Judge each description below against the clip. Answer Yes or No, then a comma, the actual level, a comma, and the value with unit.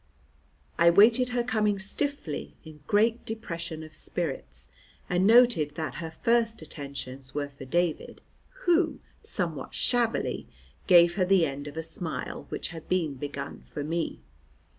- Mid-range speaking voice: Yes, medium, 170 Hz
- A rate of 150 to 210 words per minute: No, average, 140 wpm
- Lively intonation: Yes, wide, 6.6 semitones